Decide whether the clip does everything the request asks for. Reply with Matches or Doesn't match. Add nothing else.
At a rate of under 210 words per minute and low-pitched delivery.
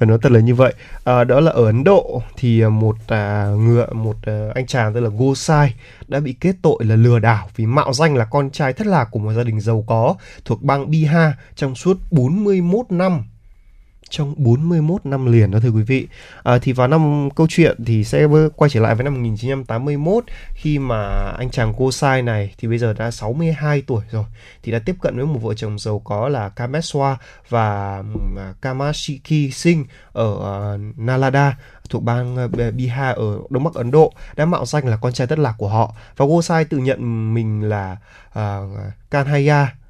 Matches